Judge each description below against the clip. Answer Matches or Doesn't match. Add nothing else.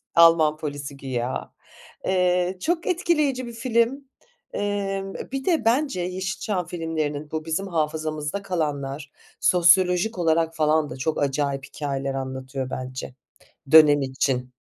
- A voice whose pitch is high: Doesn't match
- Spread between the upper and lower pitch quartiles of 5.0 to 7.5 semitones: Matches